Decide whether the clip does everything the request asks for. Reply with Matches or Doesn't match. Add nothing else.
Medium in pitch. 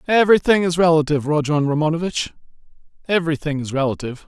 Matches